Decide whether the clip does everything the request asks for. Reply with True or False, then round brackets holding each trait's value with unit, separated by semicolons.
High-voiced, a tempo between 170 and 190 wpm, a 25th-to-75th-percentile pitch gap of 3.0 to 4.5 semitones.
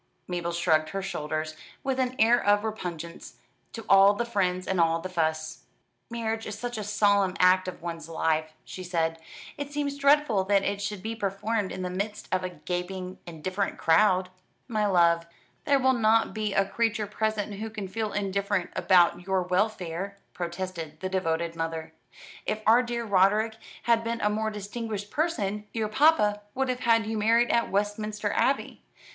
True (200 Hz; 175 wpm; 3.6 semitones)